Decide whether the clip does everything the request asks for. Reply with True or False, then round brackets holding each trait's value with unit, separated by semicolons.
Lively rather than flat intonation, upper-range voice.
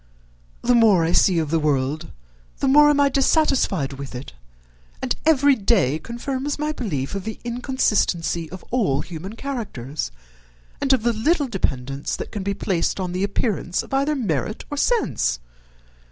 True (8.8 semitones; 205 Hz)